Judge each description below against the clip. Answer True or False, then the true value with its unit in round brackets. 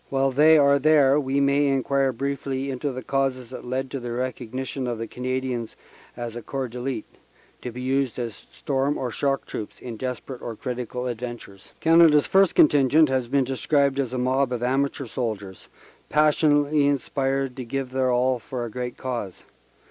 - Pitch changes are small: True (2.0 semitones)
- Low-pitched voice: True (130 Hz)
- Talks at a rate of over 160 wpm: True (180 wpm)